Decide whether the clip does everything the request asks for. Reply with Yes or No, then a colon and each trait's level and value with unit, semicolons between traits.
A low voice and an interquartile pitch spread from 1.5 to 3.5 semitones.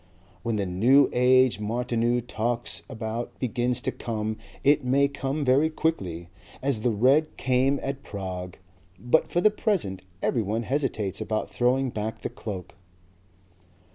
No: low, 120 Hz; average, 3.9 semitones